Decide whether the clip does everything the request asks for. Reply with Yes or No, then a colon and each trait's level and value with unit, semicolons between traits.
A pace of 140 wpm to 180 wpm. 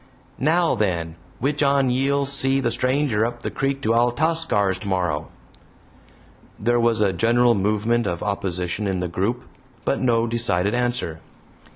Yes: average, 145 wpm